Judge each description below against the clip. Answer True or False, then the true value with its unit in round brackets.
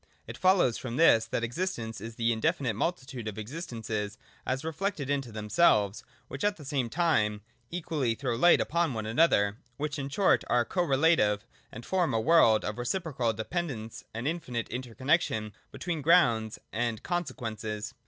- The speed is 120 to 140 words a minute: False (165 wpm)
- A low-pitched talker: True (125 Hz)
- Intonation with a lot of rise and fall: True (6.7 semitones)